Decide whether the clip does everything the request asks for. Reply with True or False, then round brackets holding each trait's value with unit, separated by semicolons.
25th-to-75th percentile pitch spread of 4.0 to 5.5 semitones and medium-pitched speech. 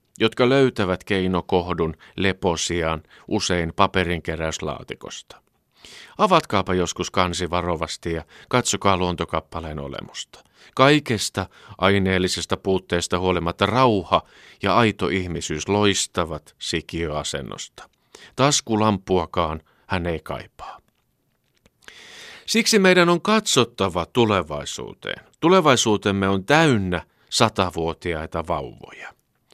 False (4.3 semitones; 95 Hz)